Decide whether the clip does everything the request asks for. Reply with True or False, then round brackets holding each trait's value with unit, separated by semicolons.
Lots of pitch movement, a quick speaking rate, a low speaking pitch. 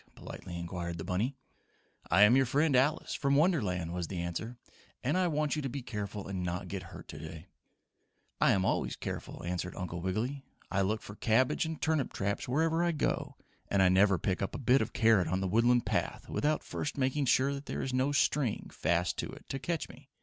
True (7.1 semitones; 210 wpm; 115 Hz)